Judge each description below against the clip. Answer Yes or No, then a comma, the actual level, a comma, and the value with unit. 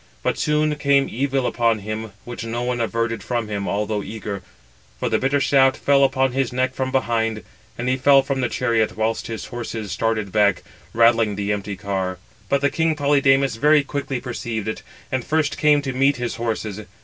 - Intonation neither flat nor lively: Yes, average, 3.8 semitones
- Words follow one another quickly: No, average, 185 wpm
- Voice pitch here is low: Yes, low, 120 Hz